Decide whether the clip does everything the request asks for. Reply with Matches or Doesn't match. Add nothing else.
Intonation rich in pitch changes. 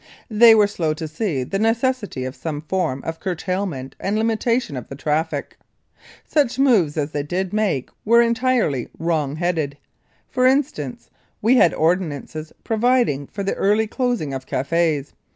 Matches